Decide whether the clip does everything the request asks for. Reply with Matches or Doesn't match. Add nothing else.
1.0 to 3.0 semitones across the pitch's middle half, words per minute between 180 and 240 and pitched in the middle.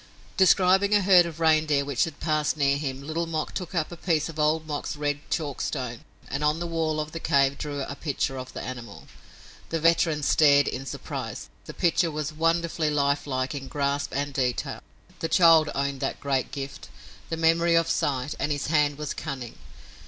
Matches